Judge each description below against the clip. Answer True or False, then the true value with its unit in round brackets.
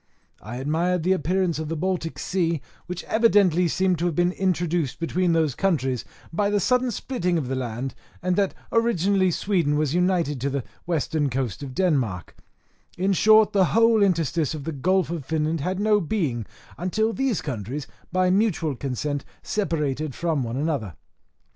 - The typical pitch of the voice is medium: True (170 Hz)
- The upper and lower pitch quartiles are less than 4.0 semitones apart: False (4.7 semitones)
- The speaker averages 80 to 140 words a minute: False (165 wpm)